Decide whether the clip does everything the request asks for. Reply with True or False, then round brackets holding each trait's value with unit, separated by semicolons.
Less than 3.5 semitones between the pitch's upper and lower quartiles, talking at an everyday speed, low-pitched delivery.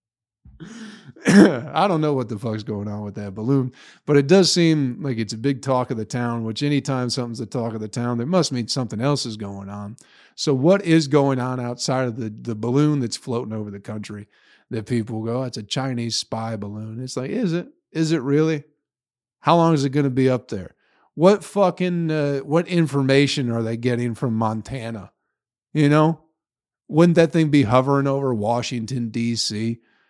False (4.6 semitones; 195 wpm; 130 Hz)